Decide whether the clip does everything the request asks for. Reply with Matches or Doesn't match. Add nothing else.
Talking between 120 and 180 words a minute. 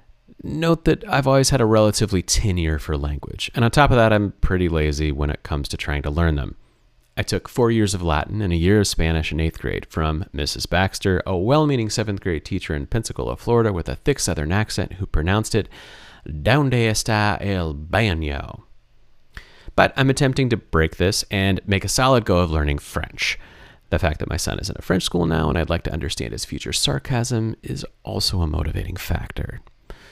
Doesn't match